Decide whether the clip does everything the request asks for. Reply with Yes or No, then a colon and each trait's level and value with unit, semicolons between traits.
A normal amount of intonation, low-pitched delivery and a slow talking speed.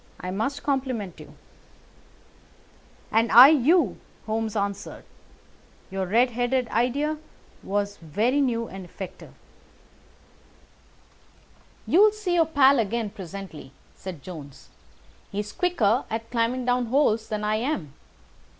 No: average, 4.9 semitones; high, 230 Hz; slow, 115 wpm